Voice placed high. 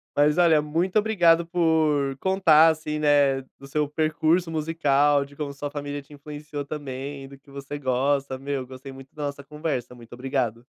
No: medium, 145 Hz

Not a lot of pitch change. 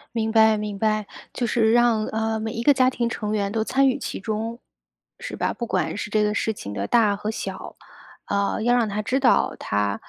Yes: narrow, 2.0 semitones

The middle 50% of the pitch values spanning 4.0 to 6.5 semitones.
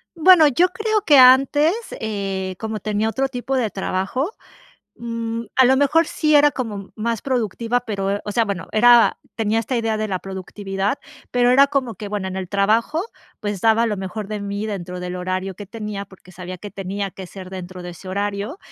Yes: average, 4.3 semitones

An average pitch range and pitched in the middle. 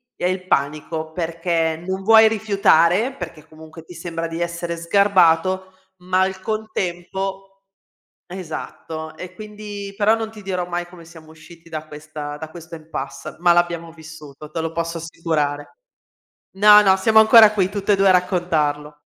Yes: average, 3.3 semitones; medium, 175 Hz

